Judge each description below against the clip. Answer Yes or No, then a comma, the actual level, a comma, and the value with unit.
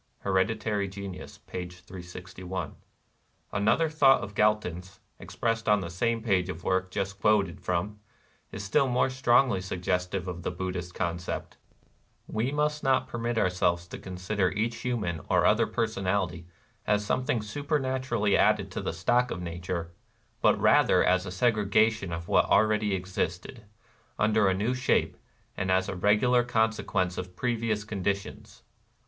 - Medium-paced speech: Yes, average, 155 wpm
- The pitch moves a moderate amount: Yes, average, 3.8 semitones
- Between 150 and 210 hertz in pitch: No, low, 100 Hz